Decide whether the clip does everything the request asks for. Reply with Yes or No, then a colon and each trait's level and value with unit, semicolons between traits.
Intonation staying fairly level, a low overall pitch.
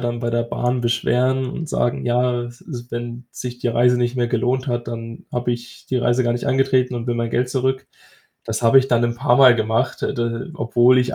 Yes: narrow, 1.2 semitones; low, 120 Hz